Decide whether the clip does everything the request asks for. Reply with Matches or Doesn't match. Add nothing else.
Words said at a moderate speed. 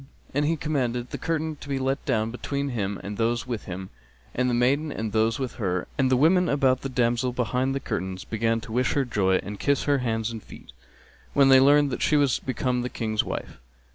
Doesn't match